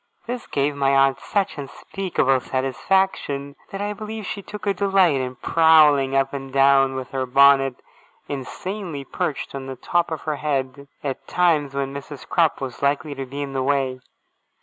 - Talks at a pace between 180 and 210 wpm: No, average, 170 wpm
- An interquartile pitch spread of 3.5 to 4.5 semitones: Yes, average, 3.8 semitones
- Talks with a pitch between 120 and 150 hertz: Yes, medium, 140 Hz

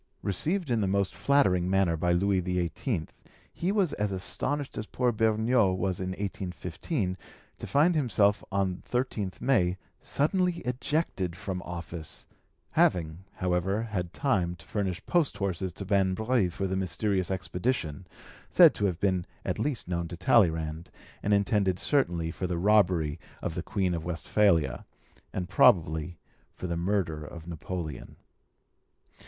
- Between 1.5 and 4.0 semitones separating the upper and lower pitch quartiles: Yes, average, 3.6 semitones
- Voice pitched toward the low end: Yes, very low, 95 Hz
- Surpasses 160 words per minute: No, average, 145 wpm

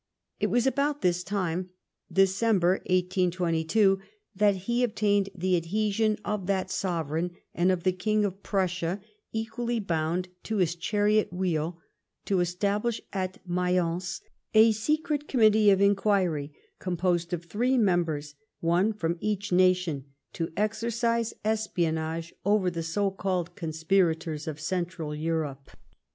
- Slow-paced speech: Yes, slow, 125 wpm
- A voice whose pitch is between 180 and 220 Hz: Yes, medium, 185 Hz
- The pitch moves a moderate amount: Yes, average, 3.6 semitones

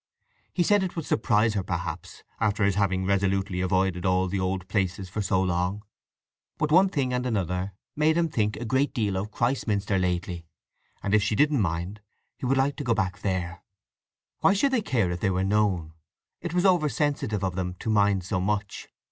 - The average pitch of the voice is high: No, low, 100 Hz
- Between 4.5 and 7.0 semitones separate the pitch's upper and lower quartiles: Yes, average, 5.2 semitones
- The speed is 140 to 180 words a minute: No, average, 200 wpm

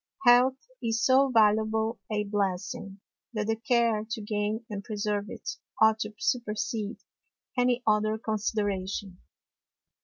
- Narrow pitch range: Yes, narrow, 1.7 semitones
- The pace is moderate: No, slow, 120 wpm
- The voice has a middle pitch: No, high, 215 Hz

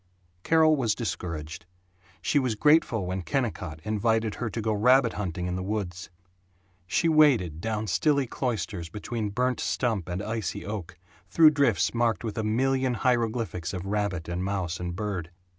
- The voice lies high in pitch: No, low, 110 Hz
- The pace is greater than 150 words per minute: Yes, average, 160 wpm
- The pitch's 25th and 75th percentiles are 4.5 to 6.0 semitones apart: Yes, average, 5.3 semitones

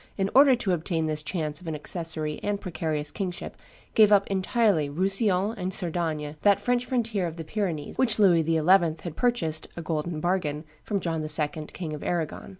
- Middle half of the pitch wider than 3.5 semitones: Yes, average, 4.1 semitones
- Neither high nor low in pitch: Yes, medium, 175 Hz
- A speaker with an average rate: Yes, average, 180 wpm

